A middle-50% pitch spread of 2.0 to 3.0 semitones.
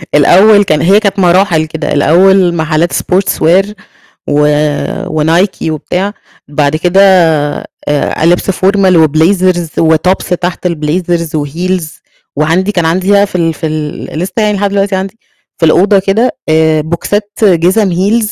No: average, 3.6 semitones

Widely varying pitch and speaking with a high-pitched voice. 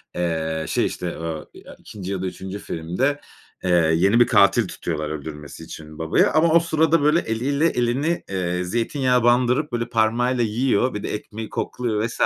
No: wide, 6.4 semitones; low, 110 Hz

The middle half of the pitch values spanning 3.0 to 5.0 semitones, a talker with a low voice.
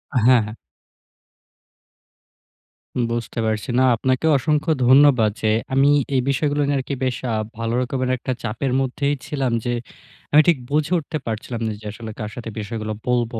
Yes: average, 3.7 semitones; low, 125 Hz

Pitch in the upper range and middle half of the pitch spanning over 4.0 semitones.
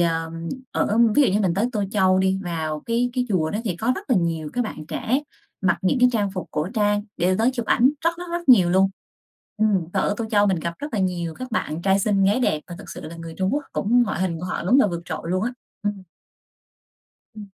Yes: high, 195 Hz; average, 4.7 semitones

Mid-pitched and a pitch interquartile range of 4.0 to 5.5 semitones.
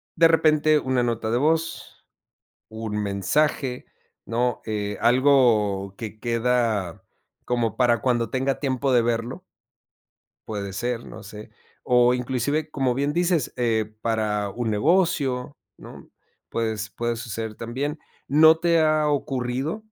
No: low, 125 Hz; average, 4.4 semitones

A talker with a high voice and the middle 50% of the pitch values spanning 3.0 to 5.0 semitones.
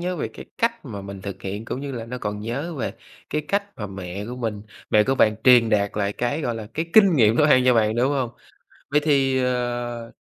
No: low, 120 Hz; average, 4.5 semitones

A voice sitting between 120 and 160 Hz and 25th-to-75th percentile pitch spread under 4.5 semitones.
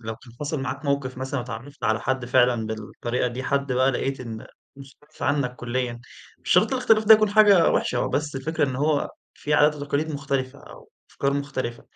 Yes: low, 135 Hz; average, 2.8 semitones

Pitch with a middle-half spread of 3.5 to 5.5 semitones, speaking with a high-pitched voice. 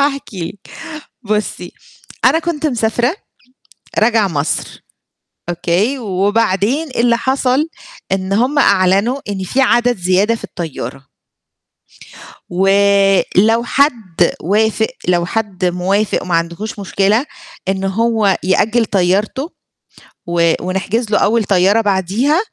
Yes: average, 4.0 semitones; high, 205 Hz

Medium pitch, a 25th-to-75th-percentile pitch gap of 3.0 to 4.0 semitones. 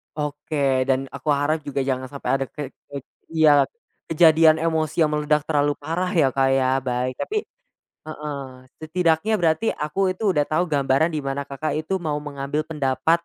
No: medium, 150 Hz; narrow, 2.6 semitones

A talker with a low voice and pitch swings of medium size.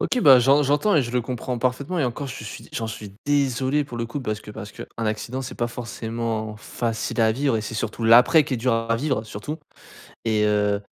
Yes: low, 120 Hz; average, 3.3 semitones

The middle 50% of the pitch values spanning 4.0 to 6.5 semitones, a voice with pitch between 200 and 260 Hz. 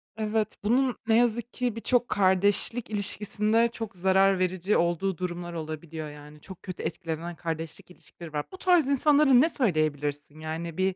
No: wide, 5.6 semitones; high, 190 Hz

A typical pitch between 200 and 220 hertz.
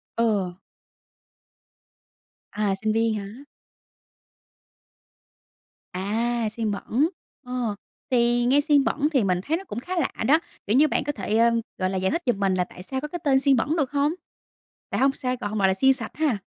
No: high, 240 Hz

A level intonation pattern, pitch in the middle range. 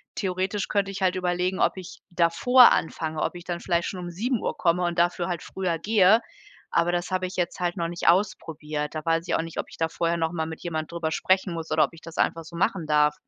Yes: narrow, 2.1 semitones; medium, 175 Hz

